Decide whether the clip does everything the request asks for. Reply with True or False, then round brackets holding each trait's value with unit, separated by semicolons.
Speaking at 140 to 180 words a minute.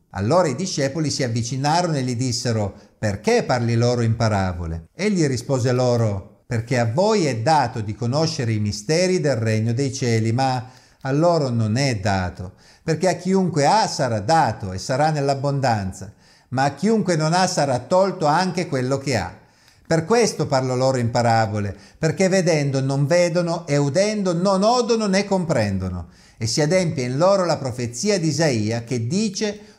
True (165 wpm)